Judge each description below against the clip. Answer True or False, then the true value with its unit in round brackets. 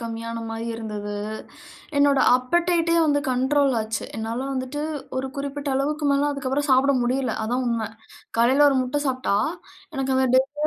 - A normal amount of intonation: True (3.4 semitones)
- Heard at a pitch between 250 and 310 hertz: True (265 Hz)